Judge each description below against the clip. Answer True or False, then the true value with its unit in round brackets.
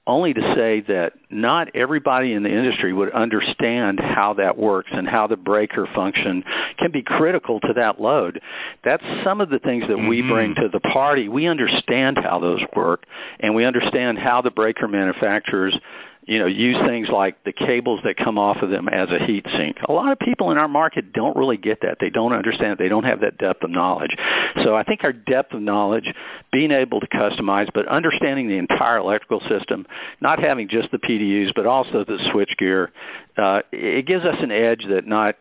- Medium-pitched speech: False (110 Hz)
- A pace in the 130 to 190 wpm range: False (205 wpm)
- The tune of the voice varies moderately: False (2.2 semitones)